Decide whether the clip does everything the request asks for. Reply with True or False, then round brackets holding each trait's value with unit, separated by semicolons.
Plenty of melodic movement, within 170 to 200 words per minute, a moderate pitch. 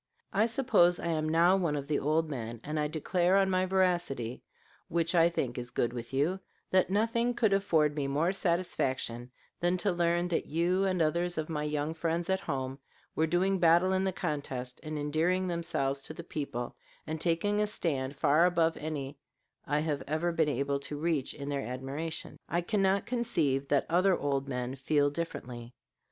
False (4.0 semitones; 185 wpm; 160 Hz)